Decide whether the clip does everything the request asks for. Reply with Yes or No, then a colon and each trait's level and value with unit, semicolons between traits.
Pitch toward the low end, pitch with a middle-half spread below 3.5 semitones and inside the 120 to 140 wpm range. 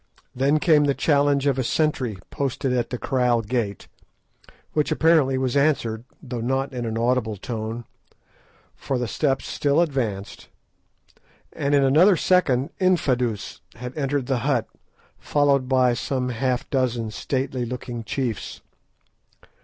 Yes: low, 130 Hz; average, 2.8 semitones; slow, 135 wpm